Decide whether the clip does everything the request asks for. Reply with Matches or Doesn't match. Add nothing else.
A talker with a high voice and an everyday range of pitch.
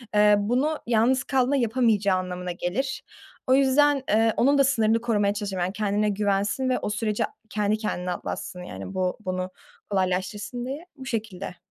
Matches